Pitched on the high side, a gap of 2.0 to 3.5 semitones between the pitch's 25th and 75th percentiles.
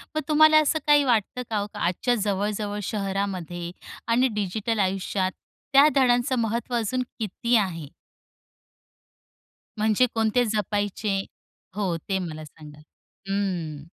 No: high, 210 Hz; average, 4.1 semitones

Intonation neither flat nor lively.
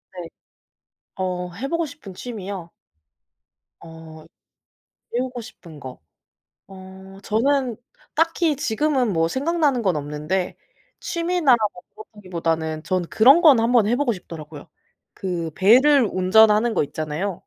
No: wide, 7.3 semitones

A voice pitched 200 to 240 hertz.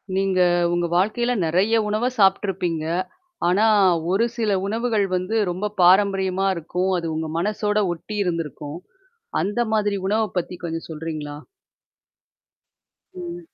No: high, 190 Hz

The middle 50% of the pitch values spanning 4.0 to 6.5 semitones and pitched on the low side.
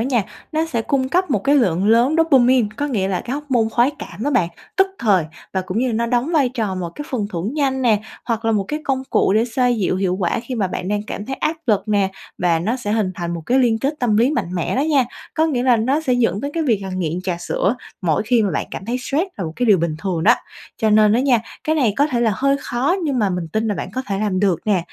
No: average, 5.2 semitones; high, 230 Hz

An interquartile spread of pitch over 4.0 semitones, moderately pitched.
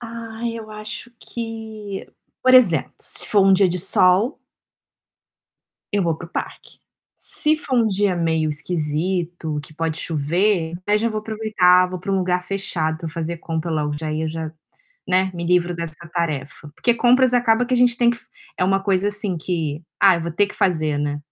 Yes: average, 4.9 semitones; medium, 180 Hz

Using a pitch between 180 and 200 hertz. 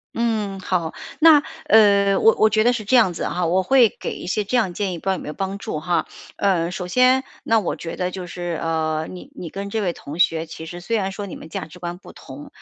Yes: high, 190 Hz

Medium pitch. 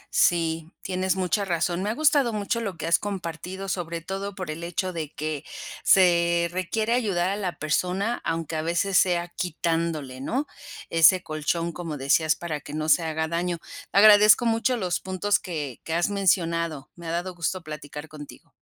Yes: medium, 175 Hz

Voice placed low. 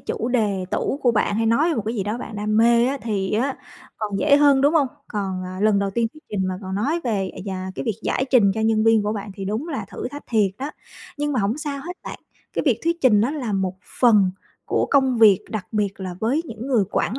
No: high, 220 Hz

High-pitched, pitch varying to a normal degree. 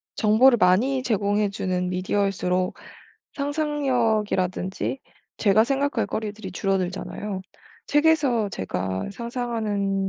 Yes: high, 210 Hz; average, 4.5 semitones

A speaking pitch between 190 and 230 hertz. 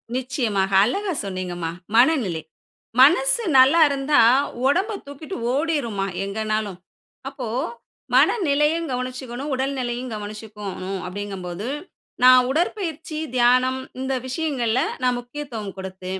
No: very high, 255 Hz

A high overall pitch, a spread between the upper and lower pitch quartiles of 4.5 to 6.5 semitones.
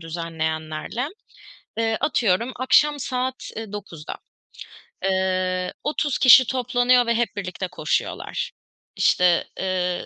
Yes: high, 200 Hz; wide, 5.6 semitones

